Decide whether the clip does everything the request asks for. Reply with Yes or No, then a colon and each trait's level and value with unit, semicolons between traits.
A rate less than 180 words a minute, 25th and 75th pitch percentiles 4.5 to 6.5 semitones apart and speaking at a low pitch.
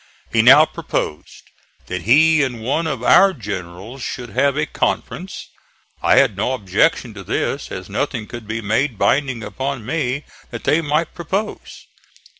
Yes: average, 155 wpm; wide, 5.6 semitones; low, 130 Hz